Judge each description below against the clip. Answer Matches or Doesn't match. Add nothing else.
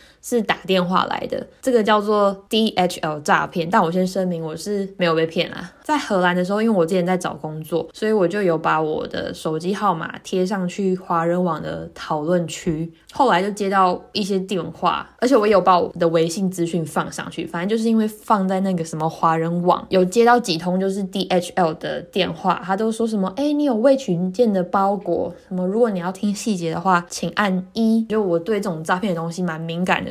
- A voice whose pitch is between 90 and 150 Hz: Doesn't match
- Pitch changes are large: Doesn't match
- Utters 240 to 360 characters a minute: Matches